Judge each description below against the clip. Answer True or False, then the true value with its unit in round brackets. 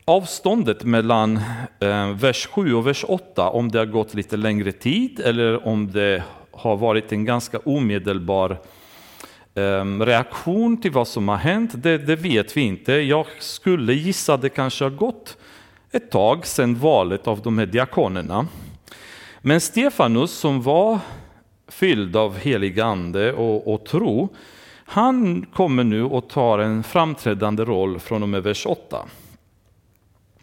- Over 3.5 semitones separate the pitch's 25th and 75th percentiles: True (5.6 semitones)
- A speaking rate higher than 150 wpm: False (145 wpm)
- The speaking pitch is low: True (115 Hz)